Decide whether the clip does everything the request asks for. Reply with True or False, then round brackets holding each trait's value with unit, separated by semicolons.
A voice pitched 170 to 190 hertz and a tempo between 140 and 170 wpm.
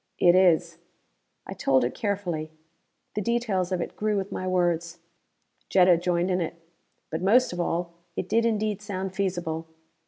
True (185 Hz; 160 wpm)